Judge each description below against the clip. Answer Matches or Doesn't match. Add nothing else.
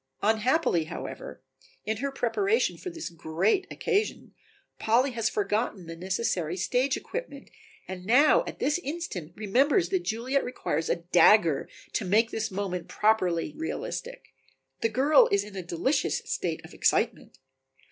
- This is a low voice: Doesn't match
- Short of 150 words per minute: Matches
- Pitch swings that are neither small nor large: Doesn't match